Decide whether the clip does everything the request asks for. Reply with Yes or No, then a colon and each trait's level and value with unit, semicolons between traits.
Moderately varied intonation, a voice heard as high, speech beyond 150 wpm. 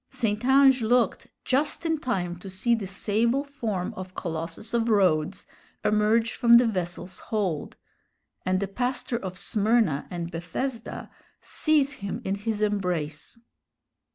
No: average, 4.6 semitones; high, 210 Hz; slow, 135 wpm